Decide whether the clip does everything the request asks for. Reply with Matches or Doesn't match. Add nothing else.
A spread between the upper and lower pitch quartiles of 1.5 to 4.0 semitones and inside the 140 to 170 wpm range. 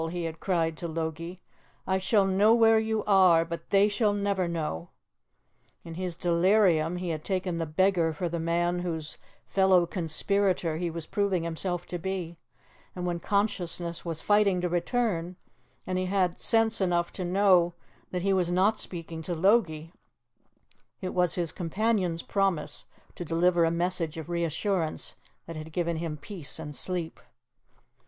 Matches